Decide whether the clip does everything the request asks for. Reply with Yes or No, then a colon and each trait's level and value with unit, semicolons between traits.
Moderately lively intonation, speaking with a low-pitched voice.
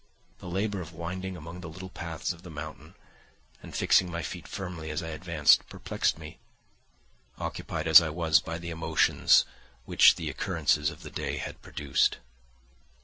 No: narrow, 2.2 semitones; very low, 85 Hz